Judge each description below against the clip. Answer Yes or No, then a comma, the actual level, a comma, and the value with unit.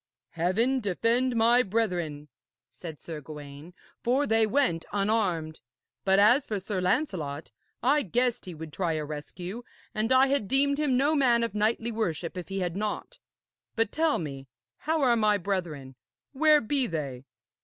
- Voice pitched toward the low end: No, high, 210 Hz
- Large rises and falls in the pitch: Yes, wide, 7.0 semitones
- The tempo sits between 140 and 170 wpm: Yes, average, 160 wpm